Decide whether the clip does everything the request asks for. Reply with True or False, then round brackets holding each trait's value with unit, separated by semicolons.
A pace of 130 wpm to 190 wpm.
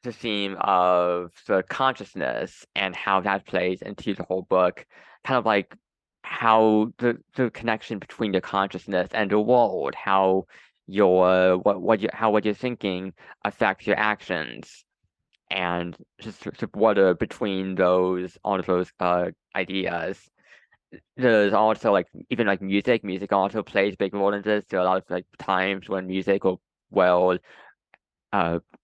True (160 wpm)